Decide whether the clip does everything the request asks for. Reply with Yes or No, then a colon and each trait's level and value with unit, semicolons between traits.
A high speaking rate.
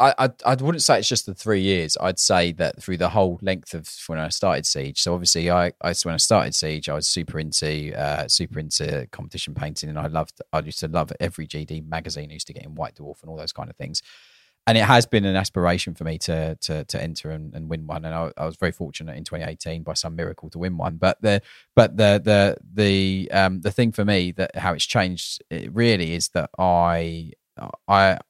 Yes: fast, 240 wpm